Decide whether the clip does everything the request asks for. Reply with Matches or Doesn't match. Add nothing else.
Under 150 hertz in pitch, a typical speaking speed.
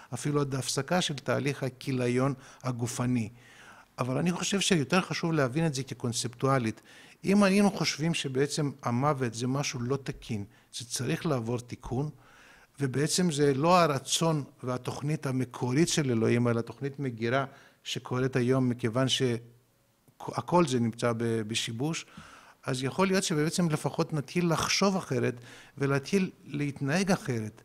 Matches